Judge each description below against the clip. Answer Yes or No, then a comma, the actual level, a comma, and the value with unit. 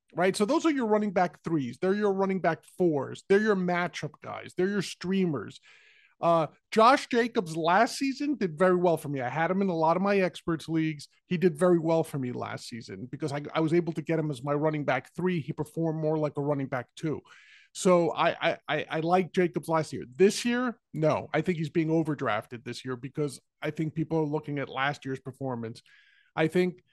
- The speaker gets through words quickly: Yes, fast, 225 wpm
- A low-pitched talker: No, medium, 165 Hz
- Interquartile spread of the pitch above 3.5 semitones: Yes, average, 3.9 semitones